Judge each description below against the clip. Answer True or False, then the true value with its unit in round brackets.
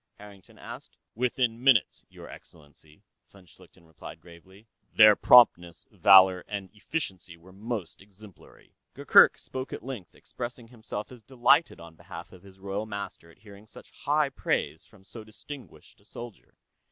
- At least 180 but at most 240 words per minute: False (150 wpm)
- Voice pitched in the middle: False (100 Hz)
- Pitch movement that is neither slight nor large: True (4.4 semitones)